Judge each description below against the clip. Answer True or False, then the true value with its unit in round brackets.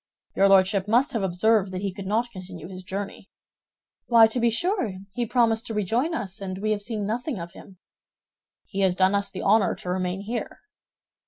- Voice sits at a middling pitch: False (200 Hz)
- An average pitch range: True (3.3 semitones)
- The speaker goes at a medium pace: True (195 wpm)